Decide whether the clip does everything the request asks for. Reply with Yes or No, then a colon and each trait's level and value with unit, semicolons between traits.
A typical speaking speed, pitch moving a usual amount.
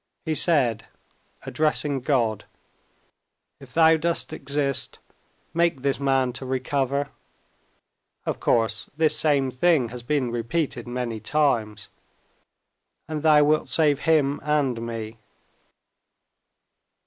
No: slow, 105 wpm; average, 3.9 semitones